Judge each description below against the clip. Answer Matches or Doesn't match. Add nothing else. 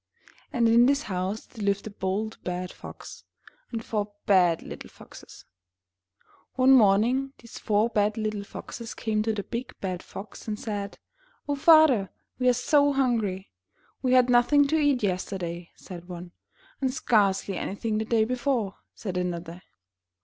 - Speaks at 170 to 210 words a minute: Doesn't match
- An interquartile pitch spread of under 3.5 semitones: Doesn't match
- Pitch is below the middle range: Doesn't match